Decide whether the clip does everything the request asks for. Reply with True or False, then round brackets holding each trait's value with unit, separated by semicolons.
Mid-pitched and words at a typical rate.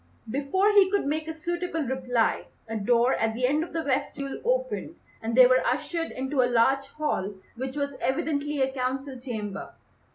False (270 Hz; 175 wpm)